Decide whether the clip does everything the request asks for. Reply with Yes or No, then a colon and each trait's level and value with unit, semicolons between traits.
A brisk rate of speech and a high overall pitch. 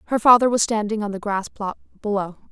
Yes: fast, 215 wpm; high, 210 Hz